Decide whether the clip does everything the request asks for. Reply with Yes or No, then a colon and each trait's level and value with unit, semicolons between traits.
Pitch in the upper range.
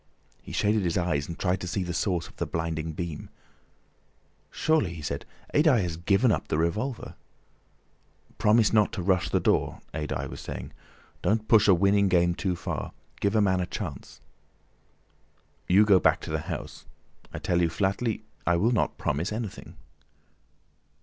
No: very low, 95 Hz